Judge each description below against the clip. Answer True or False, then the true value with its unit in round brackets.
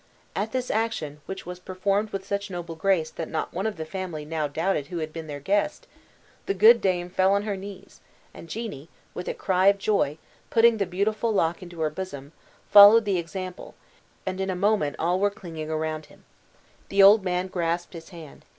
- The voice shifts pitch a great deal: False (3.6 semitones)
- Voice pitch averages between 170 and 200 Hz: True (185 Hz)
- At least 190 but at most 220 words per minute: True (200 wpm)